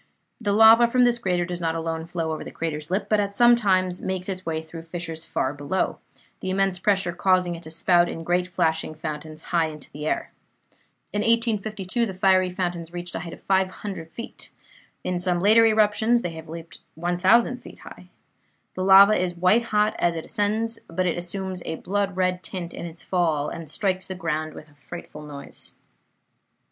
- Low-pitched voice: No, medium, 180 Hz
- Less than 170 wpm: No, average, 190 wpm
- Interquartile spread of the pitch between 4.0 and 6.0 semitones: No, average, 3.4 semitones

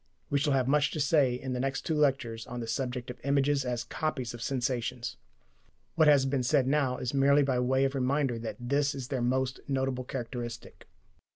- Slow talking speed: No, average, 200 wpm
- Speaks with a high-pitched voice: No, low, 130 Hz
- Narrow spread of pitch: Yes, narrow, 2.1 semitones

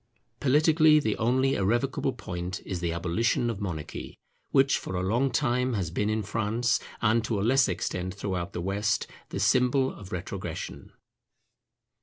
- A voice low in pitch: Yes, low, 110 Hz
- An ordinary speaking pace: Yes, average, 155 wpm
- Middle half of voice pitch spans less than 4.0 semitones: No, average, 5.3 semitones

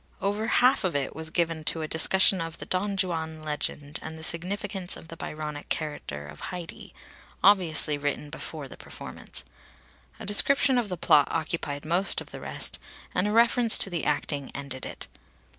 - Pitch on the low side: No, medium, 165 Hz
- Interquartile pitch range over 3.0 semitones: Yes, average, 4.0 semitones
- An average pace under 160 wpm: No, average, 175 wpm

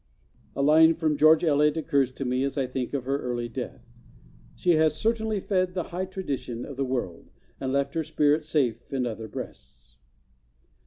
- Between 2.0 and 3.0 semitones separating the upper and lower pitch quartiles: No, average, 4.1 semitones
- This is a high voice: No, medium, 140 Hz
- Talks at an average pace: Yes, average, 180 wpm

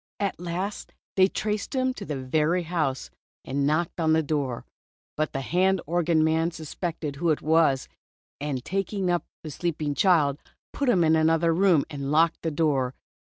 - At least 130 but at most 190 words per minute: Yes, average, 170 wpm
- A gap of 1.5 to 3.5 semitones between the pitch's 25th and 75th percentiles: Yes, average, 3.1 semitones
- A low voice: No, medium, 160 Hz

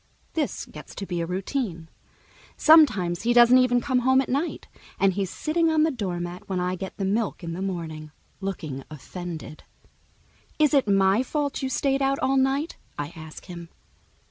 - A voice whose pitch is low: No, high, 200 Hz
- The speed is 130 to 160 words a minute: No, average, 175 wpm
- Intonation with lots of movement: Yes, wide, 7.5 semitones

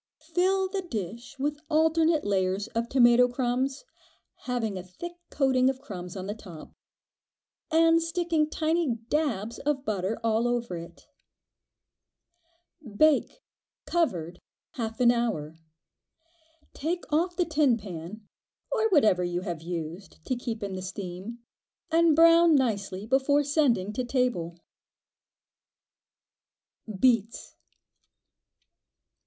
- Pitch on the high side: Yes, high, 240 Hz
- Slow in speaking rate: Yes, slow, 115 wpm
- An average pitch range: No, wide, 7.7 semitones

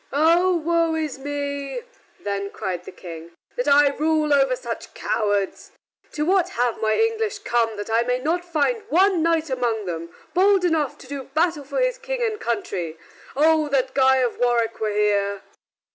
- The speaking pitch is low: No, very high, 280 Hz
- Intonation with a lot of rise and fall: Yes, wide, 6.7 semitones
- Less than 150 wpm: No, average, 175 wpm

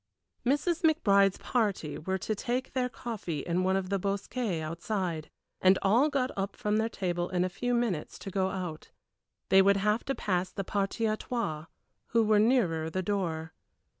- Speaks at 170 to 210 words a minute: Yes, average, 180 wpm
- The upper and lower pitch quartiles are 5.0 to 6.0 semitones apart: No, average, 4.1 semitones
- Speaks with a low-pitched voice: No, high, 195 Hz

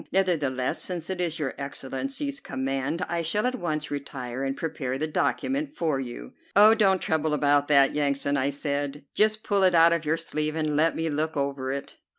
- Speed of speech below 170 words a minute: No, average, 190 wpm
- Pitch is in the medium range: Yes, medium, 155 Hz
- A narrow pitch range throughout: No, average, 4.0 semitones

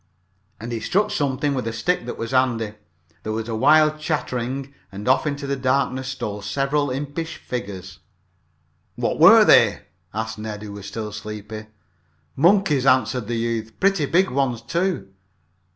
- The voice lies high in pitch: No, low, 125 Hz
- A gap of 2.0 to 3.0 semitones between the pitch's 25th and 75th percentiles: No, average, 4.5 semitones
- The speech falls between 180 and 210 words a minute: No, average, 155 wpm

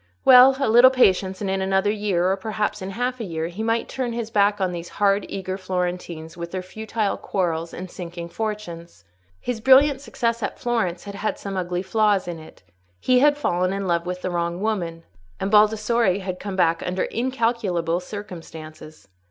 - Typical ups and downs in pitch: Yes, average, 3.9 semitones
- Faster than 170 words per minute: Yes, average, 185 wpm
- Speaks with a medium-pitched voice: No, high, 195 Hz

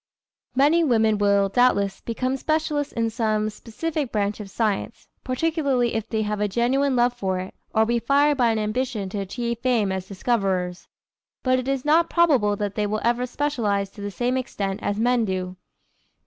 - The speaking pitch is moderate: No, high, 230 Hz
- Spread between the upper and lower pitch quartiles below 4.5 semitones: Yes, average, 4.0 semitones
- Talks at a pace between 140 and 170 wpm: No, average, 180 wpm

